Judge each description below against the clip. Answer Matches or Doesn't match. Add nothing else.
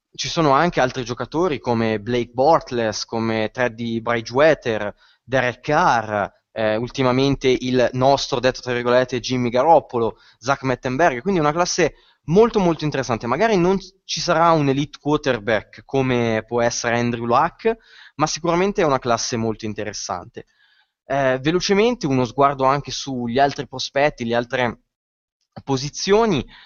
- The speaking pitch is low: Matches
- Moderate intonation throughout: Matches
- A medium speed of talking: Matches